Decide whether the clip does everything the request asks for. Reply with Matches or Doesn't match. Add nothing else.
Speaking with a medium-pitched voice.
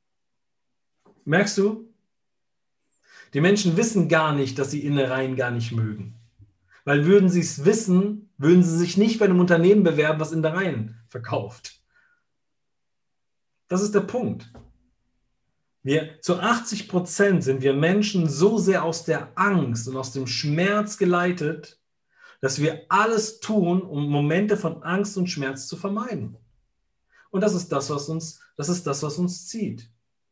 Matches